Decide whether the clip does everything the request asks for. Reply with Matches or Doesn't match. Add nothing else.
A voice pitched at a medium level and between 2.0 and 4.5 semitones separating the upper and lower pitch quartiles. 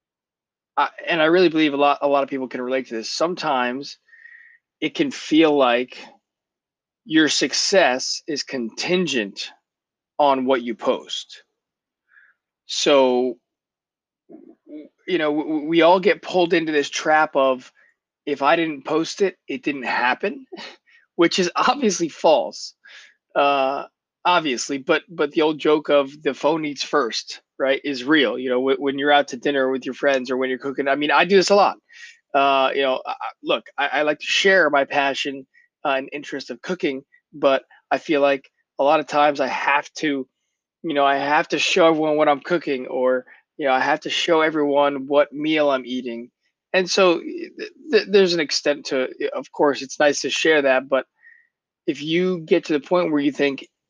Matches